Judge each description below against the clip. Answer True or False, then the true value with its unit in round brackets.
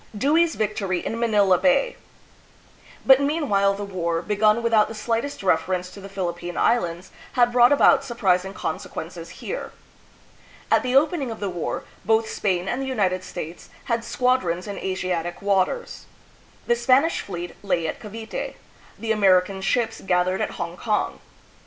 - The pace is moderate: True (150 wpm)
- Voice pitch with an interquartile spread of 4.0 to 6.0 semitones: True (4.6 semitones)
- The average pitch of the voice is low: False (205 Hz)